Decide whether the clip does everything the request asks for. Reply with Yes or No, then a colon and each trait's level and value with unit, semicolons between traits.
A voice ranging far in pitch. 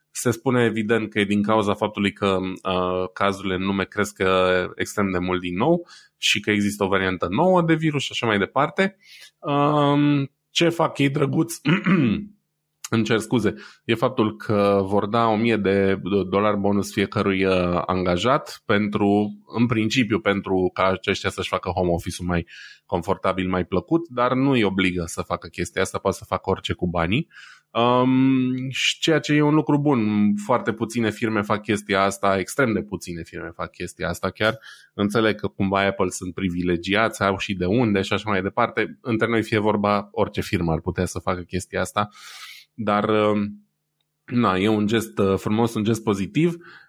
No: average, 3.8 semitones